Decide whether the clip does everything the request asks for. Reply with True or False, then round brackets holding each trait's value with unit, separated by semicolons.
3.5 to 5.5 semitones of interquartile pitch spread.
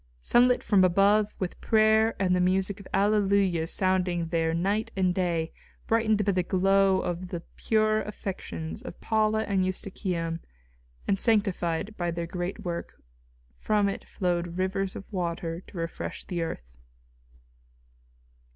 False (3.0 semitones)